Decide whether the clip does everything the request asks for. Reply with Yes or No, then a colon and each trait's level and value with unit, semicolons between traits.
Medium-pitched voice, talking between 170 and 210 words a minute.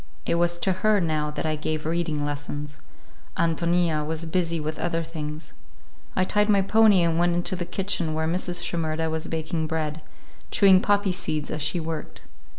Yes: medium, 165 Hz; average, 175 wpm